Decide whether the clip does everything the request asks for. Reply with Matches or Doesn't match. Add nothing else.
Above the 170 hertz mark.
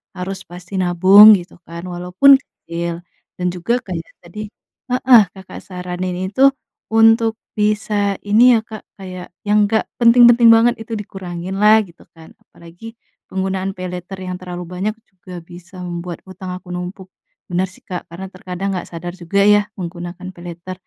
Matches